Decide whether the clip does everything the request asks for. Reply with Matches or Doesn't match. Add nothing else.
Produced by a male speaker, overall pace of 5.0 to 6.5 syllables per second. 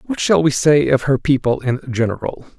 Matches